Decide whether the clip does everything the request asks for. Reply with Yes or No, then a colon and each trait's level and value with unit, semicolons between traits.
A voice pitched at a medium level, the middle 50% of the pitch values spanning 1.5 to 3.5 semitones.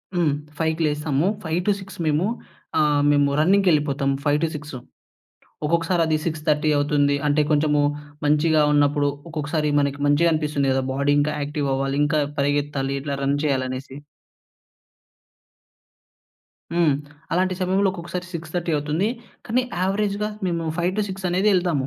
Yes: medium, 150 Hz; average, 3.2 semitones